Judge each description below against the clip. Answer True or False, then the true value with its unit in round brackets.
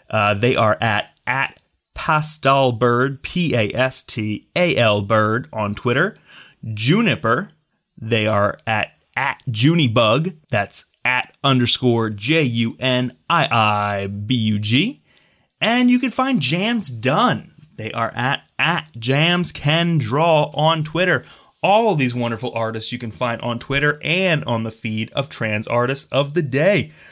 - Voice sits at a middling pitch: False (125 Hz)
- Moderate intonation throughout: False (5.7 semitones)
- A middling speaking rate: False (120 wpm)